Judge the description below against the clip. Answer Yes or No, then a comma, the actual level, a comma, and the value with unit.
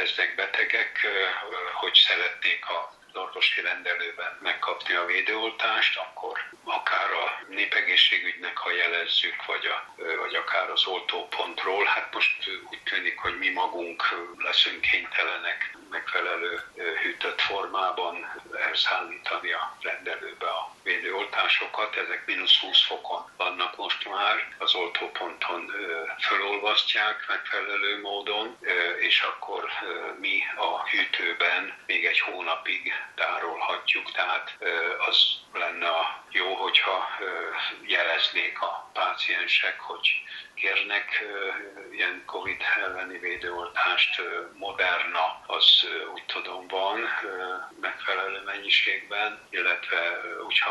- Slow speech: Yes, slow, 100 wpm